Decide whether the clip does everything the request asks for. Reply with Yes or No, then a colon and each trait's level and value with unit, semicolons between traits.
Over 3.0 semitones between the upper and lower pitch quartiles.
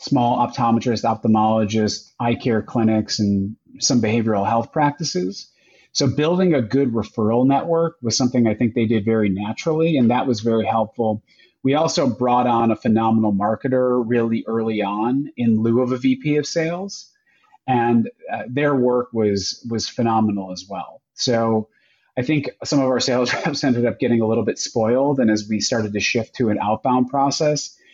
Yes: average, 3.5 semitones